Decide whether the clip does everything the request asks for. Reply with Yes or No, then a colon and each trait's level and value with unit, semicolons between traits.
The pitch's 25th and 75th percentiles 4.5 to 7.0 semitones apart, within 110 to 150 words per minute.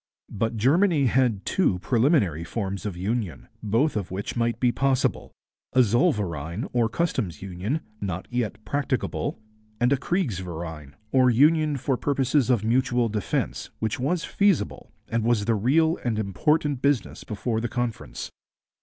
Yes: average, 5.1 semitones; average, 145 wpm